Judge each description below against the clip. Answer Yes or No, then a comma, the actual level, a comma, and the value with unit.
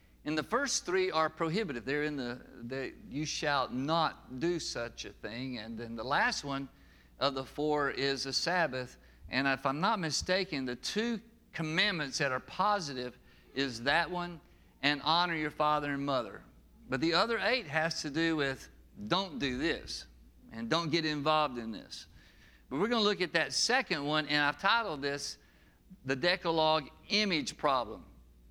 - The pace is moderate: Yes, average, 175 wpm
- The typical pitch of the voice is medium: Yes, medium, 150 Hz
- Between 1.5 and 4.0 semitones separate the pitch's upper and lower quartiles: No, average, 4.4 semitones